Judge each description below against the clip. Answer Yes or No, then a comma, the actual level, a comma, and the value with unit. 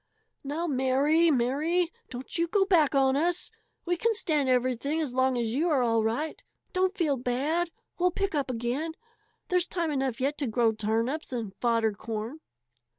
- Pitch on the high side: Yes, very high, 275 Hz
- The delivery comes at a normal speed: Yes, average, 170 wpm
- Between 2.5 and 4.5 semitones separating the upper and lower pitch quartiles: No, wide, 5.4 semitones